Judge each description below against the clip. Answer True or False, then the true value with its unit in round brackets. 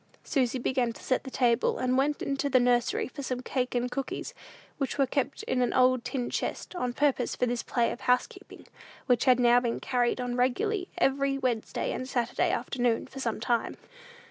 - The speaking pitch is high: True (250 Hz)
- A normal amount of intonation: False (1.8 semitones)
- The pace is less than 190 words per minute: False (195 wpm)